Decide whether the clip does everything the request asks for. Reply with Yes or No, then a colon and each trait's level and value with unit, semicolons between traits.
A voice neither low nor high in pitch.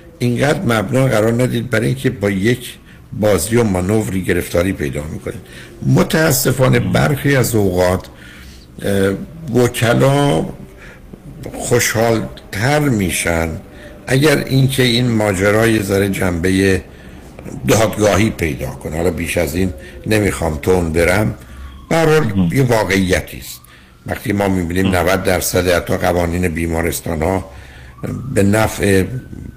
No: low, 100 Hz